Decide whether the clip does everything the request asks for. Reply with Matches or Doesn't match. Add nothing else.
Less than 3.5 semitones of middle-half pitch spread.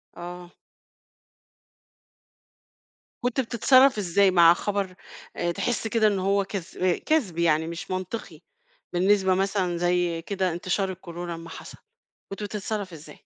Matches